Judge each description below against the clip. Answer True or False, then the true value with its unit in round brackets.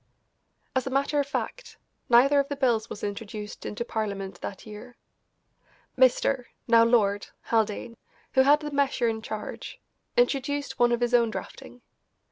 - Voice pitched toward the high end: True (240 Hz)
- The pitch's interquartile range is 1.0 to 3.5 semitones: False (4.0 semitones)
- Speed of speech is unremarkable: True (150 wpm)